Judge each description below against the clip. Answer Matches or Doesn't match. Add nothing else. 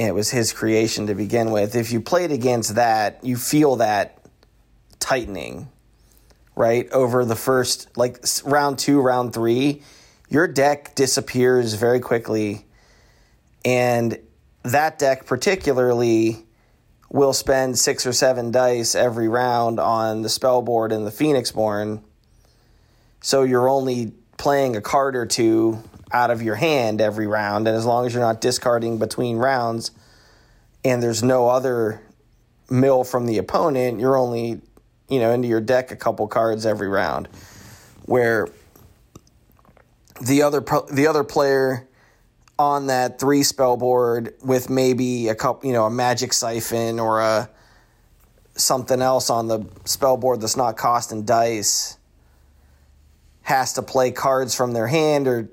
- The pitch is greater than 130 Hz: Doesn't match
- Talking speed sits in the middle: Matches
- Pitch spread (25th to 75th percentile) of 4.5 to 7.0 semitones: Doesn't match